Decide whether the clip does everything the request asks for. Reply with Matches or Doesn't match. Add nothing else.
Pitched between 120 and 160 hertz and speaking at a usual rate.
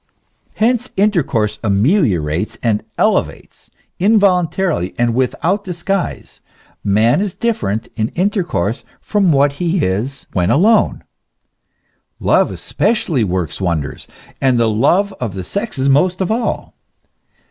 Doesn't match